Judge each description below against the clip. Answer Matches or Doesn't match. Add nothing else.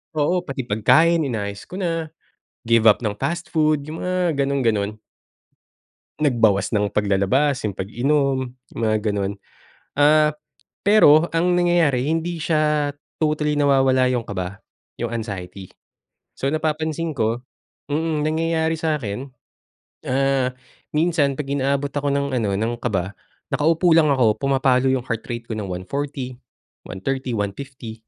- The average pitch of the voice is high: Doesn't match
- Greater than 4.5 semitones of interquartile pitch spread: Matches